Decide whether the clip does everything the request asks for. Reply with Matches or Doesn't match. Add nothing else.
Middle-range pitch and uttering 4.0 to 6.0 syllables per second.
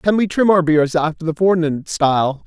Matches